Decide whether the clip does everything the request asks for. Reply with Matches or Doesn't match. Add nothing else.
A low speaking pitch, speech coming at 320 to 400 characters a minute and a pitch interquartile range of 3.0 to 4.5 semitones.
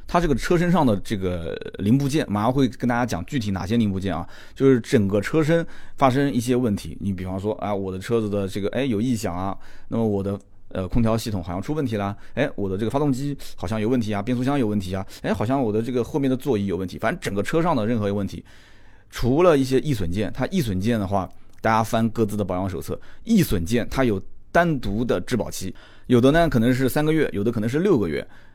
Doesn't match